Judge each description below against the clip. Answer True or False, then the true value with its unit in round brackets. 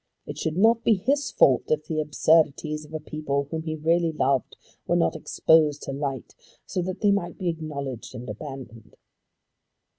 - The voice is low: False (155 Hz)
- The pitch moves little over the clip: False (3.2 semitones)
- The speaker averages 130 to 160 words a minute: False (175 wpm)